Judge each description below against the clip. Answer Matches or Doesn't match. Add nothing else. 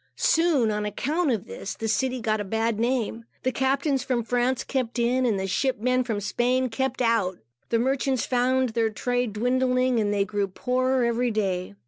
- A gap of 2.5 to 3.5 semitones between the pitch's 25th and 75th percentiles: Matches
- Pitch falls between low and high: Doesn't match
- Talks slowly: Doesn't match